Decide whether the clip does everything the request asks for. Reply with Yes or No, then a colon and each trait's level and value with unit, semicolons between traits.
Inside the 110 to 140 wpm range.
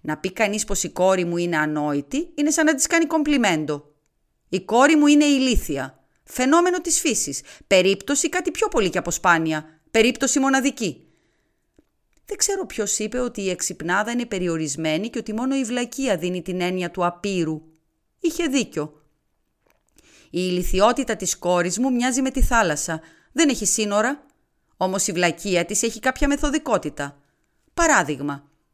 No: average, 150 wpm